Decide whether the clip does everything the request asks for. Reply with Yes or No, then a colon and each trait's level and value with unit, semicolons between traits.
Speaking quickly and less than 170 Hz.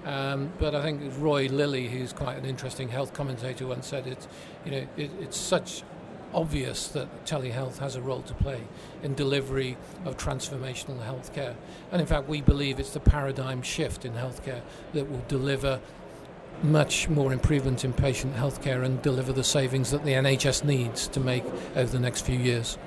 No: average, 180 wpm; low, 135 Hz